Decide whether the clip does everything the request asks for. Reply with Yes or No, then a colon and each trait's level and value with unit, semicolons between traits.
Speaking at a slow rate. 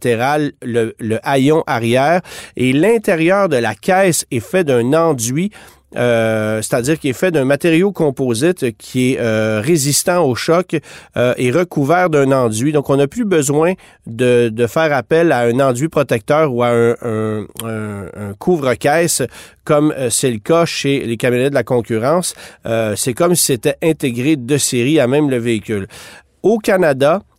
No: average, 165 wpm